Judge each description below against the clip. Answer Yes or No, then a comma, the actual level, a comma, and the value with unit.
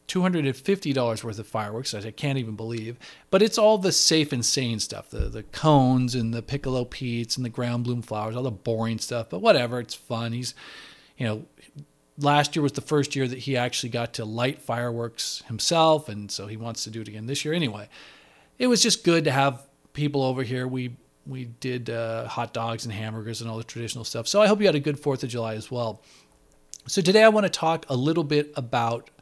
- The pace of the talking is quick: Yes, fast, 220 wpm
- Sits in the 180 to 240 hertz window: No, low, 125 Hz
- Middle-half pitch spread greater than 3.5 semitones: Yes, average, 4.0 semitones